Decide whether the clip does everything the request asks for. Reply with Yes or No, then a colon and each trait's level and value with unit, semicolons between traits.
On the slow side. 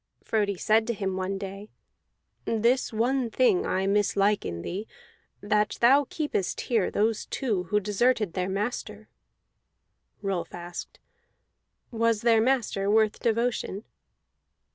Yes: slow, 120 wpm